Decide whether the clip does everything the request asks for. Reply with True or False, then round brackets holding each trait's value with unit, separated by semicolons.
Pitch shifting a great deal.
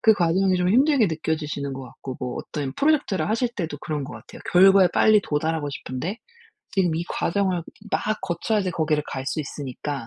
False (5.0 semitones)